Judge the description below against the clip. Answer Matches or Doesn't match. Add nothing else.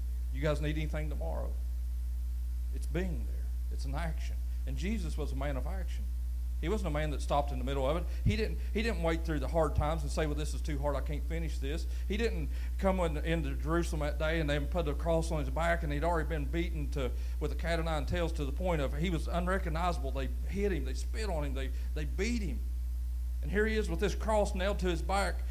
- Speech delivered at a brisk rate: Matches